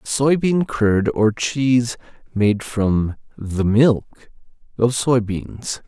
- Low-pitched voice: Yes, low, 115 Hz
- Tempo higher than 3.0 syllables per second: No, 2.7 syllables/s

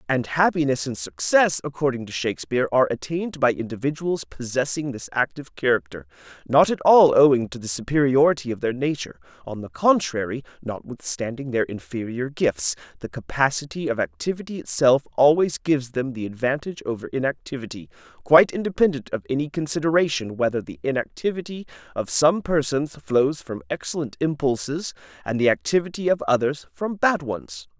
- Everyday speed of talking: Yes, average, 145 wpm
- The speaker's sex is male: Yes, male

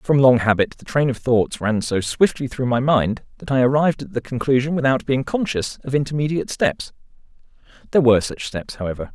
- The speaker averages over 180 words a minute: Yes, average, 195 wpm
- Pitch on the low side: Yes, low, 130 Hz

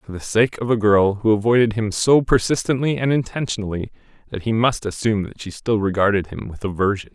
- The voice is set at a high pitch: No, low, 110 Hz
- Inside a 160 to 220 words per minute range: Yes, average, 200 wpm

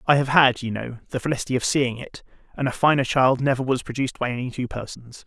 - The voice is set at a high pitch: No, low, 130 Hz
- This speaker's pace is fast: Yes, fast, 240 wpm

